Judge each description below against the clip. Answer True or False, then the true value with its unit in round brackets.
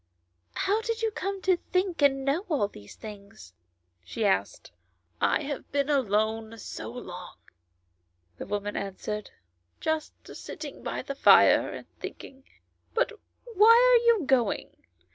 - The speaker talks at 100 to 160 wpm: True (145 wpm)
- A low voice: False (265 Hz)